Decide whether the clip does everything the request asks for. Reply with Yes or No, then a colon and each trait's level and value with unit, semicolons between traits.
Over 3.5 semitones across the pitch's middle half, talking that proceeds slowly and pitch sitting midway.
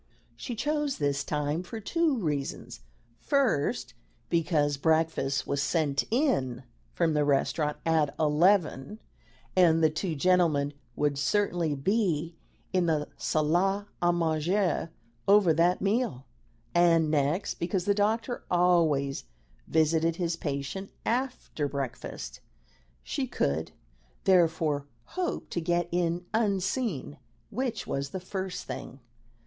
Yes: average, 4.7 semitones; slow, 115 wpm; medium, 165 Hz